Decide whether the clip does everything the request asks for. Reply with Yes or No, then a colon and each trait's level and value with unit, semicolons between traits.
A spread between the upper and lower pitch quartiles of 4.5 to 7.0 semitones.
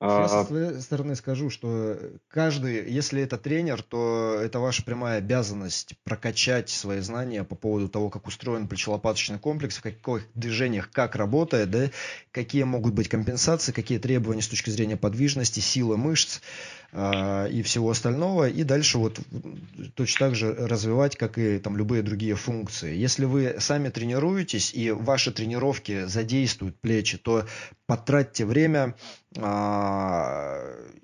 No: average, 3.8 semitones